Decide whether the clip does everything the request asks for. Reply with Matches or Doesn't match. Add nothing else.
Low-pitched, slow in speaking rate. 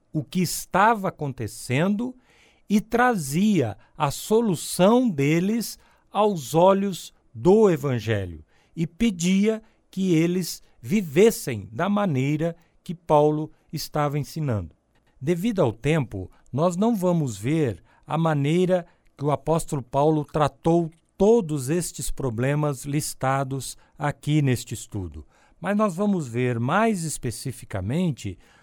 Doesn't match